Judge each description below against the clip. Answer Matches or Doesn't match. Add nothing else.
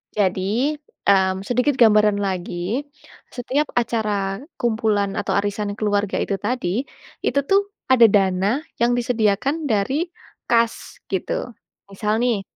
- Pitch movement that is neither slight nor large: Matches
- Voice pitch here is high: Matches